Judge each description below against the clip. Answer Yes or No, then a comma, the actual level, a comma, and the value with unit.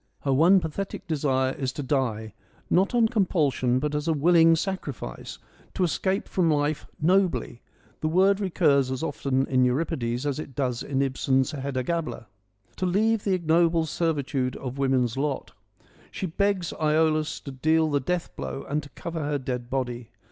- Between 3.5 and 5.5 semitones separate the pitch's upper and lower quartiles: Yes, average, 4.3 semitones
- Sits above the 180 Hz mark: No, medium, 150 Hz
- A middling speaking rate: Yes, average, 170 wpm